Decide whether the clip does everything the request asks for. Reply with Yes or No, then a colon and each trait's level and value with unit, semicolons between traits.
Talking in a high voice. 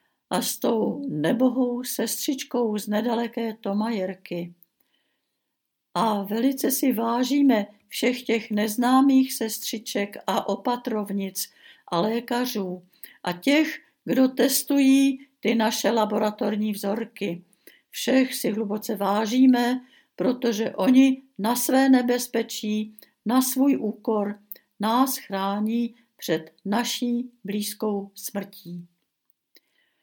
Yes: high, 230 Hz